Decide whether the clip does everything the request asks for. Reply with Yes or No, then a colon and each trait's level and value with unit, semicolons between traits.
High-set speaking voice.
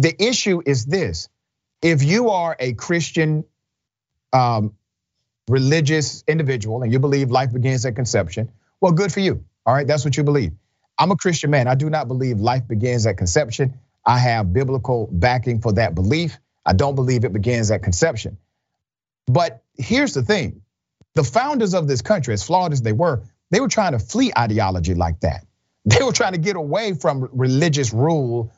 No: low, 130 Hz